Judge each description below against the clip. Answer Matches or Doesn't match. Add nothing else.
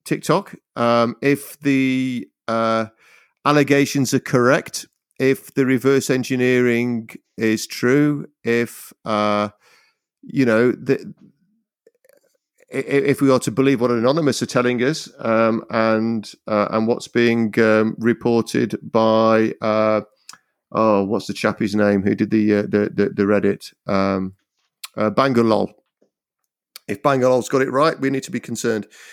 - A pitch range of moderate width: Matches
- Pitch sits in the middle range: Doesn't match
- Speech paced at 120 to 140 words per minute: Matches